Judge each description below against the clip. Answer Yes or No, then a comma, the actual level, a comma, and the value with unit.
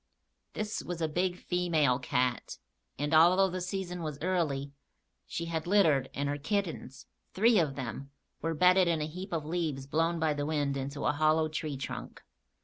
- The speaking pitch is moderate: Yes, medium, 160 Hz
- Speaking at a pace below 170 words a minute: No, average, 175 wpm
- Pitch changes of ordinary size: Yes, average, 3.7 semitones